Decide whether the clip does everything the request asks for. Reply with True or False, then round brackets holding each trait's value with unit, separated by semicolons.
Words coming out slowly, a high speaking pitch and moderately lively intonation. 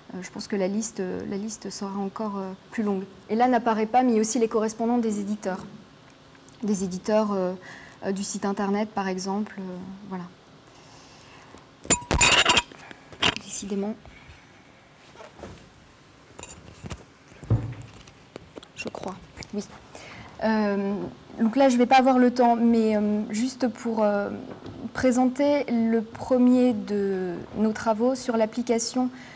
True (125 wpm; 215 Hz; 3.0 semitones)